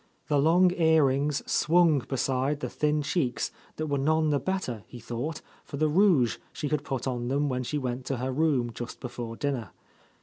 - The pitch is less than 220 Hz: Yes, medium, 140 Hz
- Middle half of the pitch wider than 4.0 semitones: No, average, 3.7 semitones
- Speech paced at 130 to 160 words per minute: No, average, 190 wpm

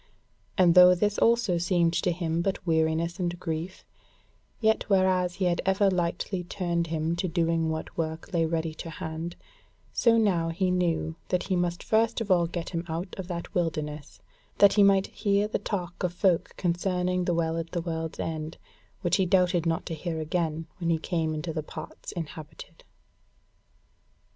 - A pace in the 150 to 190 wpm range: Yes, average, 175 wpm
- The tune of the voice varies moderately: No, narrow, 2.1 semitones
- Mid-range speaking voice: Yes, medium, 170 Hz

